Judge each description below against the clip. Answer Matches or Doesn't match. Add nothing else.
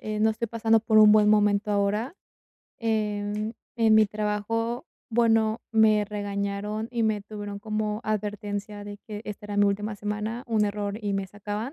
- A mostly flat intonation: Matches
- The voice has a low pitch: Doesn't match